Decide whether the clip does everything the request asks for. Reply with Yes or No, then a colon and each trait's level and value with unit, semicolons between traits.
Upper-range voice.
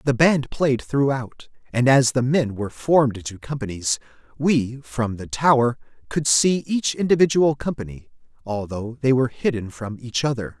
No: low, 130 Hz